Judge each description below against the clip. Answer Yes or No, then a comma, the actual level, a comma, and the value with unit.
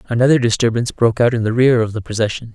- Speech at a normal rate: No, fast, 235 wpm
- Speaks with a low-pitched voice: Yes, low, 115 Hz